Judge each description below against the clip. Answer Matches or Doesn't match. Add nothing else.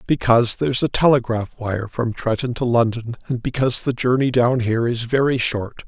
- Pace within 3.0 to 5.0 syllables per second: Doesn't match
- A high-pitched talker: Doesn't match